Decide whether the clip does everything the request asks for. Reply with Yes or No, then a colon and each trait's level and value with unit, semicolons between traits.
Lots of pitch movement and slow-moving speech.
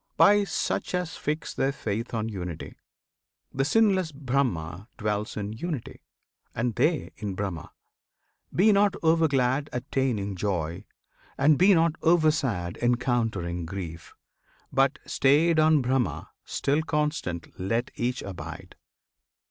Yes: wide, 7.4 semitones; slow, 125 wpm